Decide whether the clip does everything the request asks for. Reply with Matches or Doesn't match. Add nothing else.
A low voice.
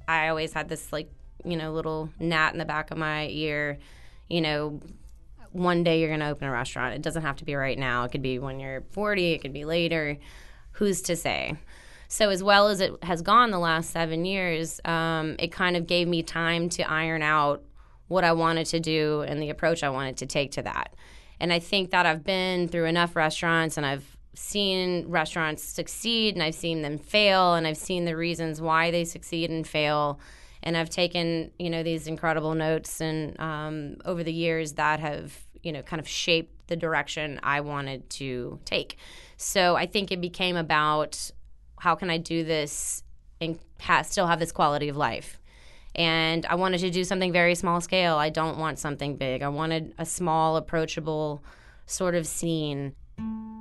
Doesn't match